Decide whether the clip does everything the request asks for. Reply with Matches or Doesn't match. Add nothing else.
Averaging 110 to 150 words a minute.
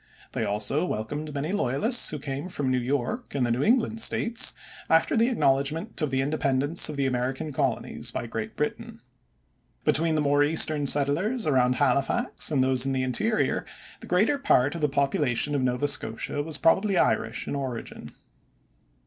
Doesn't match